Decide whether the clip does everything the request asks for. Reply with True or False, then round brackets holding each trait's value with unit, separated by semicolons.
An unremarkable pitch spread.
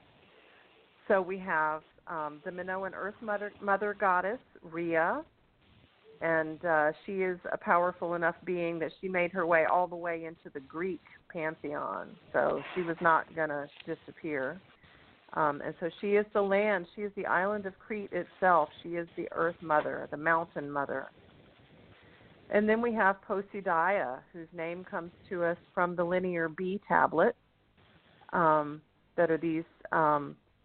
True (3.0 semitones)